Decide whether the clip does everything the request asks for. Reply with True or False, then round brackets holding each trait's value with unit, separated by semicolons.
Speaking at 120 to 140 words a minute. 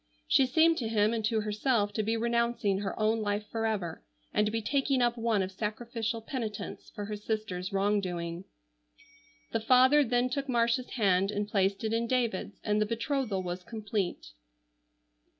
False (170 wpm)